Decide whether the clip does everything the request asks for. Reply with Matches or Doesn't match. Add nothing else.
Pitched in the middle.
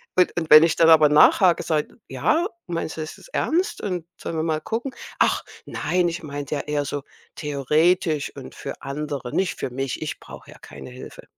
Matches